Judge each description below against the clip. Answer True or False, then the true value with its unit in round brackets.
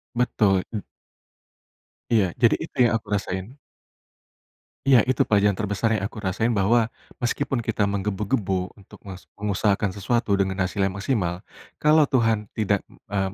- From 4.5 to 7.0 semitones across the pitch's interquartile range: False (3.1 semitones)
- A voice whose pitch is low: True (105 Hz)